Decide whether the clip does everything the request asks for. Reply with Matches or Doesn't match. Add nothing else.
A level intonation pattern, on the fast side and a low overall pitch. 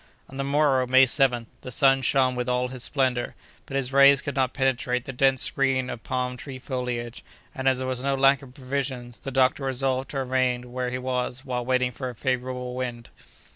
Matches